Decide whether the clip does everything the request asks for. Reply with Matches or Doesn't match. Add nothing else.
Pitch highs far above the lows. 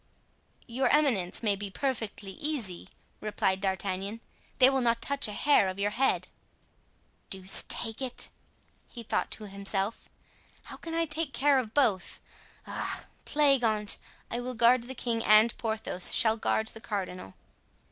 Doesn't match